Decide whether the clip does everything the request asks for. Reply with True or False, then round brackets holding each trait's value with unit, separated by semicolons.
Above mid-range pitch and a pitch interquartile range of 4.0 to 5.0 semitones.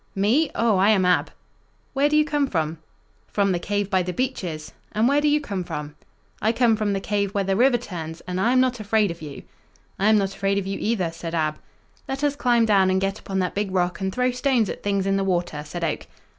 True (200 Hz; 4.5 semitones)